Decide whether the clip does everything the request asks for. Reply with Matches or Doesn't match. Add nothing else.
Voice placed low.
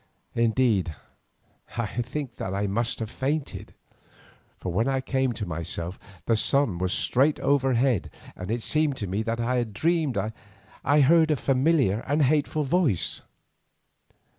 Matches